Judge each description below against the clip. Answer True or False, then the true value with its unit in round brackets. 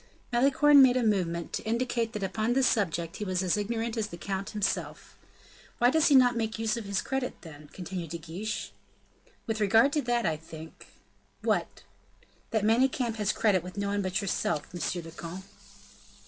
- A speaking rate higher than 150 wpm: True (190 wpm)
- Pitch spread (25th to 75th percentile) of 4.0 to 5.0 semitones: True (4.6 semitones)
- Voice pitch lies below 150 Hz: False (210 Hz)